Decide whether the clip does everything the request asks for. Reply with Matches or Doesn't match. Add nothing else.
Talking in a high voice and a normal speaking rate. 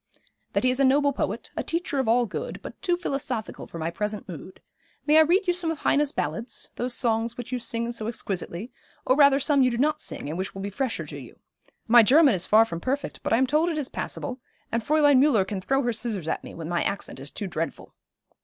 Doesn't match